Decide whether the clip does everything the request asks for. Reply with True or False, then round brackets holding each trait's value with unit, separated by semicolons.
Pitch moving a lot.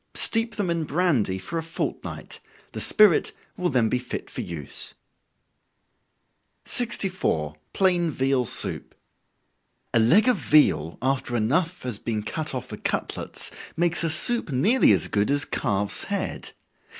True (8.0 semitones)